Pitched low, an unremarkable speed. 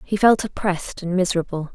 No: medium, 185 Hz; average, 170 wpm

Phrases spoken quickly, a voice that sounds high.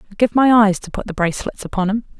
Yes: fast, 275 wpm; high, 210 Hz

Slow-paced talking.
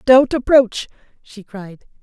Yes: slow, 120 wpm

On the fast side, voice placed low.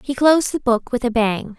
No: fast, 265 wpm; very high, 250 Hz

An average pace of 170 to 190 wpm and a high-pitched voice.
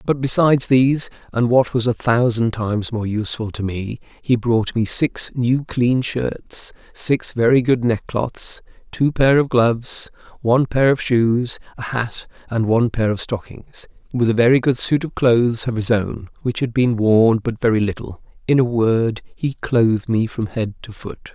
No: average, 185 wpm; low, 120 Hz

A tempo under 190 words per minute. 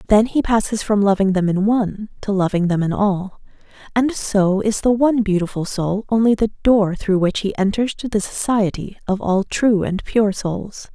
No: average, 195 wpm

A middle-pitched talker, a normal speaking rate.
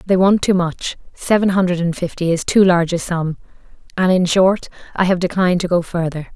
Yes: medium, 180 Hz; average, 190 wpm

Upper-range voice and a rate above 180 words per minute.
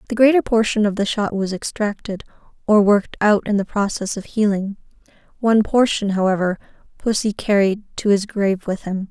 No: high, 205 Hz; average, 170 wpm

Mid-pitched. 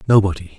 No: very low, 95 Hz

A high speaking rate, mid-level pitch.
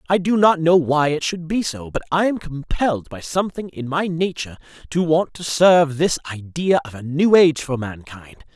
Yes: fast, 210 wpm; medium, 160 Hz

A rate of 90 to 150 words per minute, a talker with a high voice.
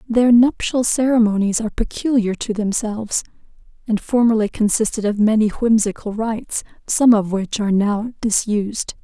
Yes: slow, 135 wpm; high, 220 Hz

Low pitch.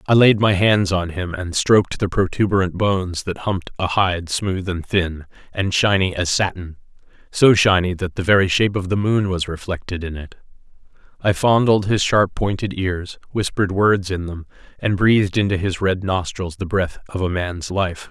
Yes: very low, 95 Hz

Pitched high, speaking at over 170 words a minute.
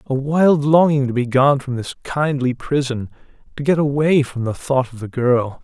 No: low, 135 Hz; average, 190 wpm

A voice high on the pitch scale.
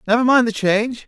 Yes: high, 230 Hz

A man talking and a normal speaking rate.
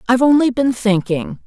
No: female; average, 165 wpm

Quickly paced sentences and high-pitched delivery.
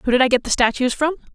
Yes: fast, 310 wpm; very high, 265 Hz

